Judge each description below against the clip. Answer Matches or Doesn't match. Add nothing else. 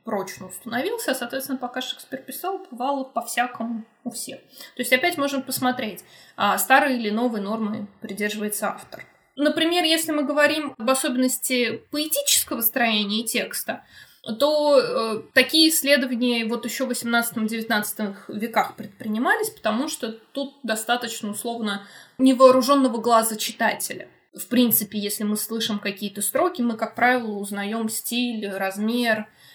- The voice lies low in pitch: Doesn't match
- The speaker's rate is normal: Matches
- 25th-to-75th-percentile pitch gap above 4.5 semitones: Doesn't match